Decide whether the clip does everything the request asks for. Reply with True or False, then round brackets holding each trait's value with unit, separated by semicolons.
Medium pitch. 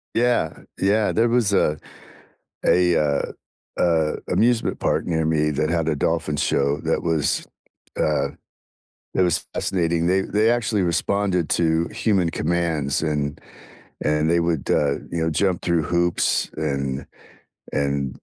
False (85 Hz)